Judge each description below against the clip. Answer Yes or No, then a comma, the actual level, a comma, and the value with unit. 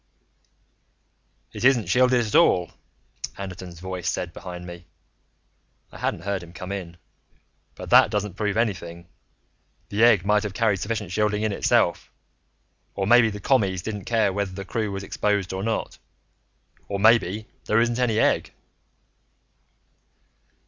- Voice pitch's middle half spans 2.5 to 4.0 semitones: Yes, average, 3.0 semitones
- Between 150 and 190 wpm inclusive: No, average, 140 wpm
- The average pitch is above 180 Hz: No, low, 100 Hz